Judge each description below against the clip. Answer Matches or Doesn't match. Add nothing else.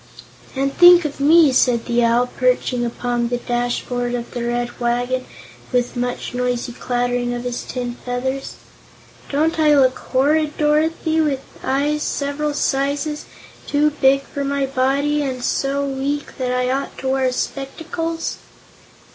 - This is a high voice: Matches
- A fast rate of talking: Doesn't match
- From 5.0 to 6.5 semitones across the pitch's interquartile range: Doesn't match